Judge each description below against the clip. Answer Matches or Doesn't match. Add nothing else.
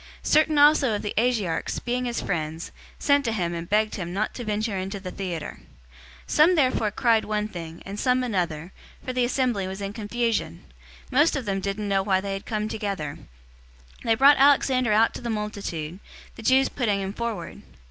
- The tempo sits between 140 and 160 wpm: Doesn't match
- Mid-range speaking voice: Doesn't match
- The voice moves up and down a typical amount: Matches